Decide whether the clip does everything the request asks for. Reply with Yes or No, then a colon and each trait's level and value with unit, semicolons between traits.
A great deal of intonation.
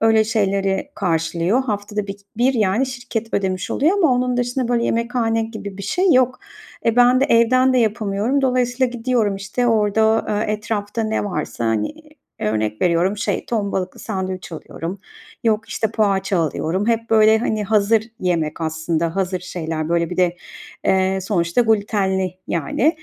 No: average, 3.9 semitones